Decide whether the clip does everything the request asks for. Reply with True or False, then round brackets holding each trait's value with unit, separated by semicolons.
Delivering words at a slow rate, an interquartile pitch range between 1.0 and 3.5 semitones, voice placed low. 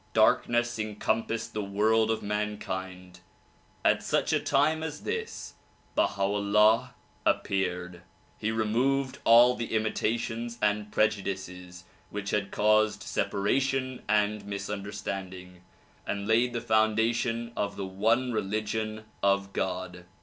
True (115 wpm; 2.7 semitones; 105 Hz)